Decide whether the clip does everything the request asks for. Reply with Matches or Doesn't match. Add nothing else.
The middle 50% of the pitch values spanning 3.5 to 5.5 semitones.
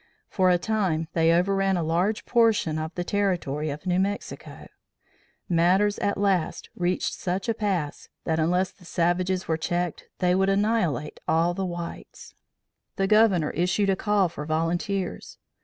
Doesn't match